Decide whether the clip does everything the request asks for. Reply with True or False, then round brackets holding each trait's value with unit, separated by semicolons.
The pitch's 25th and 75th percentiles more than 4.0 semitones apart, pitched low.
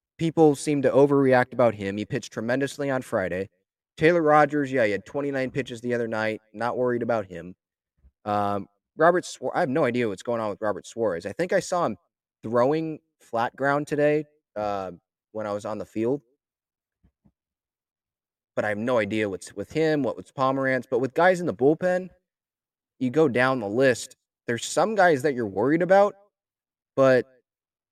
True (5.6 semitones; 125 Hz)